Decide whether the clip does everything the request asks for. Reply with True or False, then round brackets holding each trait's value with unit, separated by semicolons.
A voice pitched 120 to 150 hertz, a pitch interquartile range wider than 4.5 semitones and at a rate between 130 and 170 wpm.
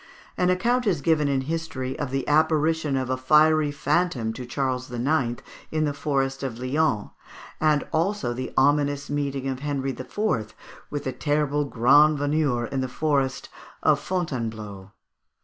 False (140 Hz; 3.1 semitones; 150 wpm)